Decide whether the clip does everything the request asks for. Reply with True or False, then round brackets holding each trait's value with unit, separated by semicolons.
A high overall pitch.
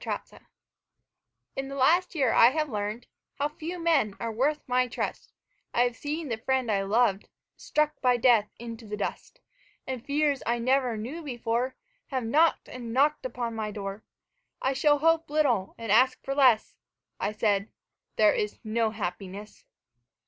True (245 Hz)